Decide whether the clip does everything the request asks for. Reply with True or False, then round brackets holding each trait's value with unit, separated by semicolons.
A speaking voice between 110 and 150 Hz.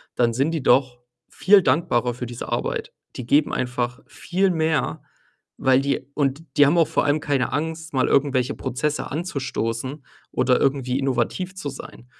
True (140 Hz)